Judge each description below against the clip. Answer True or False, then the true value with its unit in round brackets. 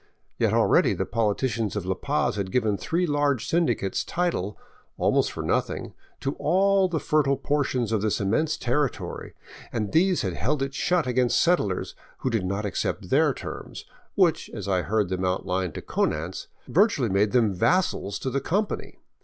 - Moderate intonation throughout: False (7.5 semitones)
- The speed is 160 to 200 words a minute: True (170 wpm)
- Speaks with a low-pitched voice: True (120 Hz)